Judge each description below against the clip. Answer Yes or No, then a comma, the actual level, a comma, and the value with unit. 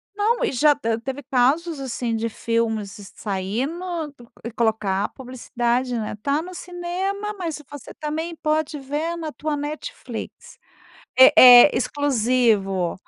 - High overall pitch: Yes, very high, 275 Hz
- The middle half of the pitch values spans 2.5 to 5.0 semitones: No, wide, 5.6 semitones